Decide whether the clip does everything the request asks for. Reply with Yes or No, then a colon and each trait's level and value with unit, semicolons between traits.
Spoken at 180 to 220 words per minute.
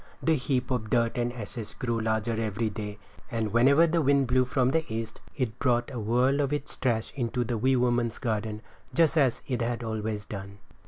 Yes: average, 200 wpm